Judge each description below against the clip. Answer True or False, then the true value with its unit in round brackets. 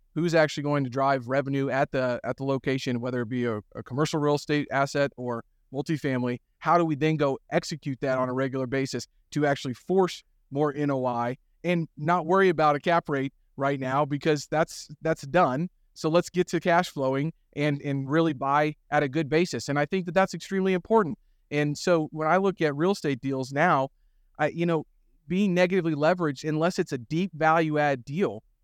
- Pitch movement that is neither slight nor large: True (3.6 semitones)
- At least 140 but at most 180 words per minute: False (200 wpm)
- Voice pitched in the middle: True (150 Hz)